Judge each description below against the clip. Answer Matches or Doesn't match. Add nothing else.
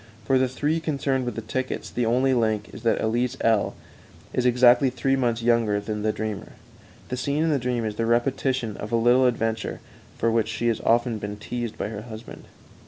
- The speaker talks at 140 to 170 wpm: Doesn't match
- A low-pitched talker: Matches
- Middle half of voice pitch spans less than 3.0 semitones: Matches